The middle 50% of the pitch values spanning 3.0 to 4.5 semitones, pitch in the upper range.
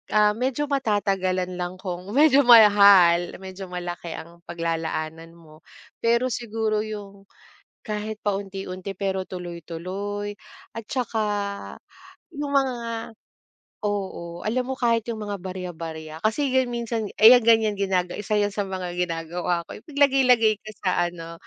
Yes: average, 4.1 semitones; high, 200 Hz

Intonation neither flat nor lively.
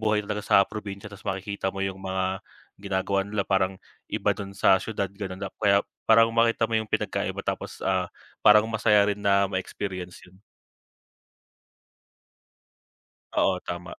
No: narrow, 1.7 semitones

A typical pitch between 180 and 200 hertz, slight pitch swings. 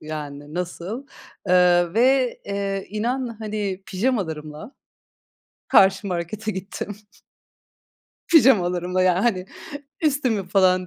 No: high, 190 Hz; average, 3.9 semitones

